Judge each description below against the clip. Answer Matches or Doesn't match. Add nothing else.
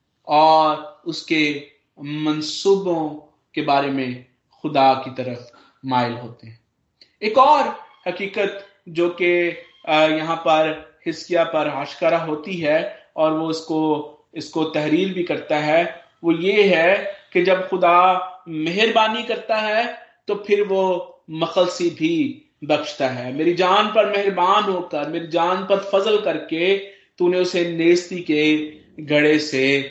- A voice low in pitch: Doesn't match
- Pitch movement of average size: Matches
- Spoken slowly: Doesn't match